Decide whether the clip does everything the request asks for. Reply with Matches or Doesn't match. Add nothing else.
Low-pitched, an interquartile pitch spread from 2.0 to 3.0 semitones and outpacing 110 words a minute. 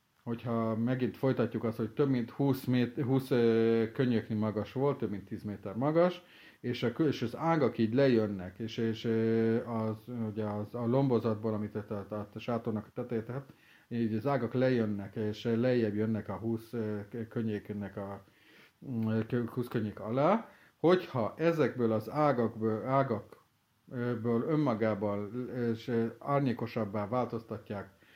Matches